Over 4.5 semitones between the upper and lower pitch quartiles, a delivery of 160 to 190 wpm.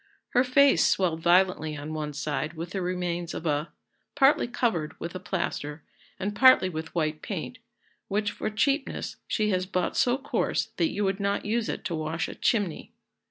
Yes: average, 4.9 semitones; average, 180 wpm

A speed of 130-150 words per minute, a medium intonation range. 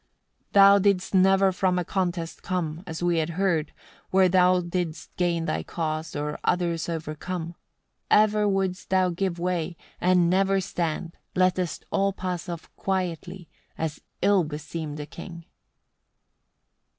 No: average, 140 wpm; narrow, 2.3 semitones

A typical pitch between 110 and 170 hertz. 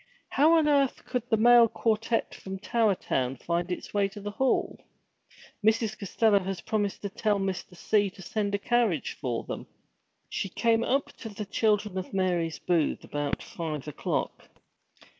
No: high, 205 Hz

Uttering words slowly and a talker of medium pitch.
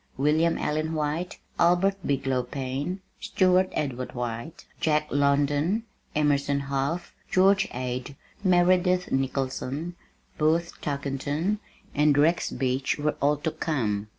Yes: slow, 110 wpm; medium, 150 Hz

